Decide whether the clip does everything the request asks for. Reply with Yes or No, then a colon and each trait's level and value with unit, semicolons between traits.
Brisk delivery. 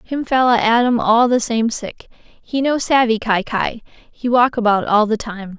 No: average, 195 wpm